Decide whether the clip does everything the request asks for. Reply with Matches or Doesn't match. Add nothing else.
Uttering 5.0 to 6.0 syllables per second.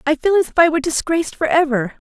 Doesn't match